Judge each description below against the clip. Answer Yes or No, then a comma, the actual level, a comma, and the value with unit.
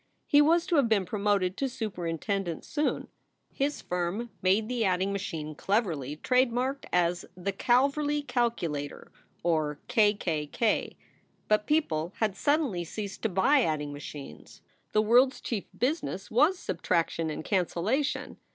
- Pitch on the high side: Yes, high, 205 Hz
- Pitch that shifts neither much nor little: No, wide, 6.6 semitones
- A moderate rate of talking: Yes, average, 145 wpm